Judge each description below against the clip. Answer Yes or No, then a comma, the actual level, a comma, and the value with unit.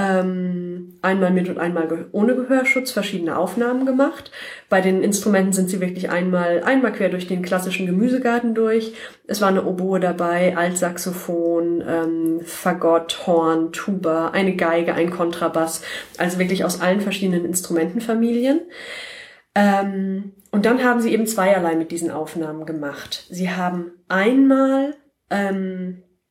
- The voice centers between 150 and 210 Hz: Yes, medium, 185 Hz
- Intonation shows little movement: No, average, 3.6 semitones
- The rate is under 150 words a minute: Yes, average, 130 wpm